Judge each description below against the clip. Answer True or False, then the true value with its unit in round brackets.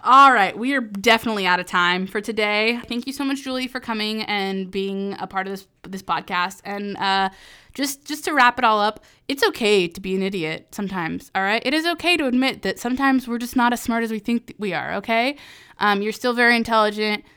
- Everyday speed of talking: False (230 wpm)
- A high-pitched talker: True (220 Hz)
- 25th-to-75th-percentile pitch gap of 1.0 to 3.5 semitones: False (4.1 semitones)